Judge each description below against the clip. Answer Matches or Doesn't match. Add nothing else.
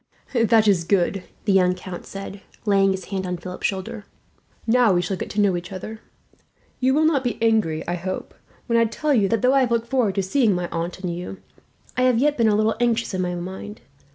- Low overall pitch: Doesn't match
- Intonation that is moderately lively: Matches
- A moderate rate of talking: Doesn't match